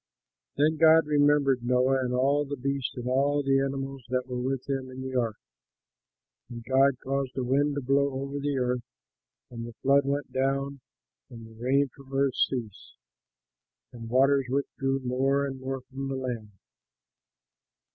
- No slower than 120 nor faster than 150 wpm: No, average, 165 wpm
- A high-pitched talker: No, low, 135 Hz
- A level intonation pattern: Yes, narrow, 1.7 semitones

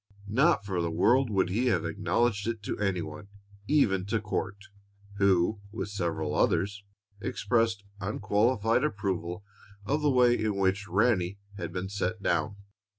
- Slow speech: No, average, 150 wpm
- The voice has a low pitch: Yes, low, 100 Hz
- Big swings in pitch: No, average, 3.1 semitones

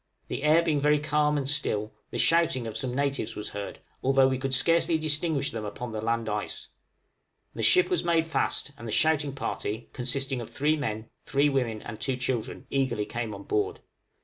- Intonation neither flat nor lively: Yes, average, 4.6 semitones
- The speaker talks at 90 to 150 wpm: No, average, 195 wpm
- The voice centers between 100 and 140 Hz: Yes, low, 135 Hz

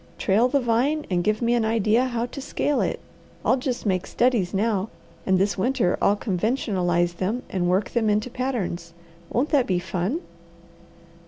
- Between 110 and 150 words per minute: No, average, 170 wpm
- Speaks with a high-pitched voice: Yes, high, 215 Hz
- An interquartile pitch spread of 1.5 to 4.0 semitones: No, average, 5.0 semitones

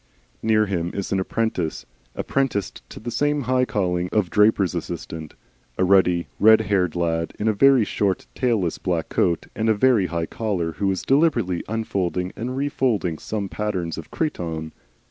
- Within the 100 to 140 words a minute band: No, average, 165 wpm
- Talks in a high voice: No, low, 100 Hz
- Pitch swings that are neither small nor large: Yes, average, 4.4 semitones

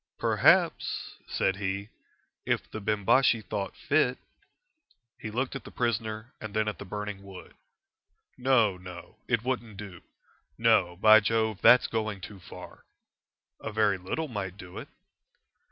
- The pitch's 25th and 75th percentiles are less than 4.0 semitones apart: Yes, average, 3.1 semitones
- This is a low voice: Yes, low, 110 Hz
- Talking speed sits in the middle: Yes, average, 145 wpm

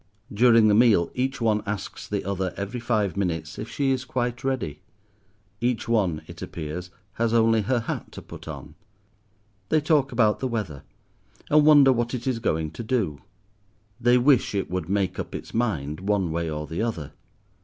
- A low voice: Yes, low, 110 Hz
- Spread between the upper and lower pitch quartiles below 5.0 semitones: No, average, 5.3 semitones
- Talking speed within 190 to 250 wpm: No, average, 180 wpm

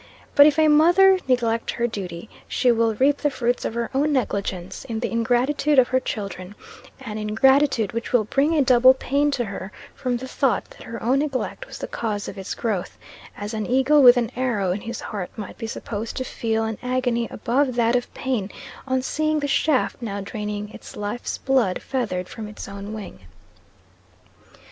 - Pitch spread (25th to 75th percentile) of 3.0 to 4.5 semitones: Yes, average, 3.9 semitones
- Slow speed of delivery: No, average, 190 wpm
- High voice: Yes, high, 240 Hz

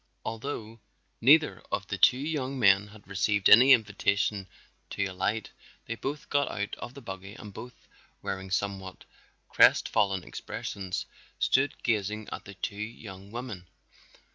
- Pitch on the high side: No, low, 105 Hz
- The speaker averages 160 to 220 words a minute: No, average, 140 wpm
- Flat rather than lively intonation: No, average, 3.8 semitones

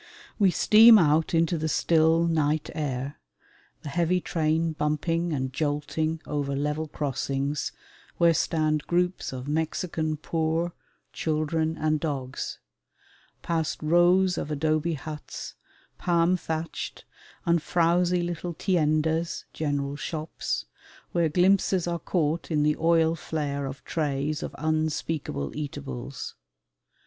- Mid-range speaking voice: Yes, medium, 155 Hz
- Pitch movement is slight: Yes, narrow, 2.2 semitones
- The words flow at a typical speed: No, slow, 115 wpm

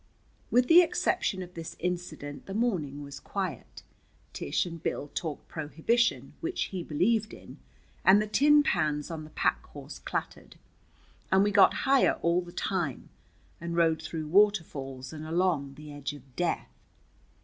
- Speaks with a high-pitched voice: No, medium, 170 Hz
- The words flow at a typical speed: Yes, average, 155 wpm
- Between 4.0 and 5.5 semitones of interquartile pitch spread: Yes, average, 4.8 semitones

